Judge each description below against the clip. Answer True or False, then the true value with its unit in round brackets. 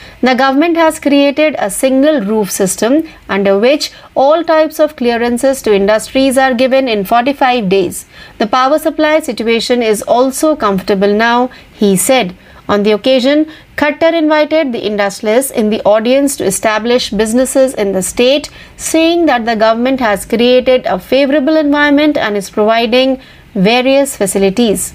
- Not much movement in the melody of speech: False (5.2 semitones)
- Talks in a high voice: True (255 Hz)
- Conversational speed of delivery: False (150 wpm)